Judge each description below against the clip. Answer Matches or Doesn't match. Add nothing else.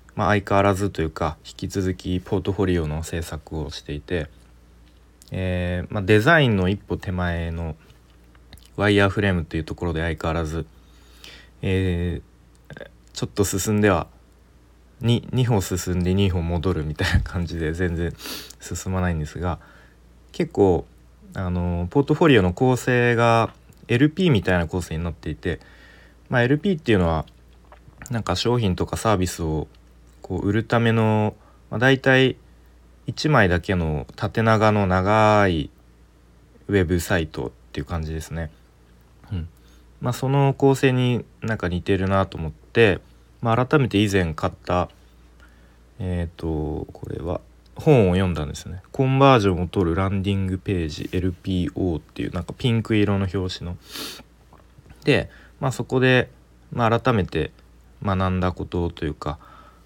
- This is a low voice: Matches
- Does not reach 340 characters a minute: Matches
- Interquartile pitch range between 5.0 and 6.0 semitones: Matches